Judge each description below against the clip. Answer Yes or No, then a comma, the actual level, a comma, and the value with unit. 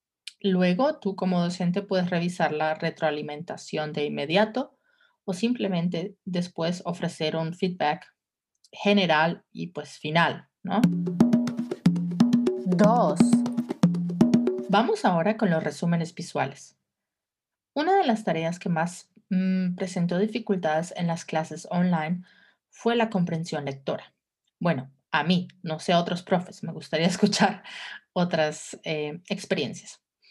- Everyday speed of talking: No, slow, 115 wpm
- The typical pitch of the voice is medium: Yes, medium, 180 Hz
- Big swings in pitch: No, average, 3.9 semitones